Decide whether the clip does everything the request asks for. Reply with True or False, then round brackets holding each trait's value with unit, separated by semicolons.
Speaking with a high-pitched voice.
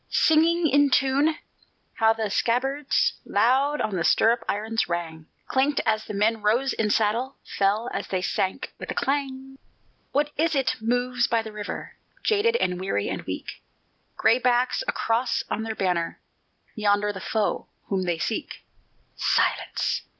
True (230 Hz)